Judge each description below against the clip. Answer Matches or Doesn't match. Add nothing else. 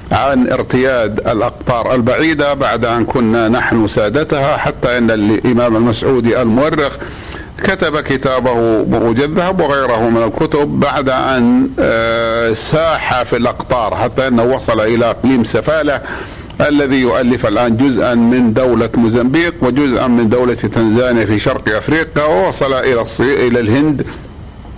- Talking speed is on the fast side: Doesn't match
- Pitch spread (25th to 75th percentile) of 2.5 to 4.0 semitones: Matches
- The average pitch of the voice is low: Matches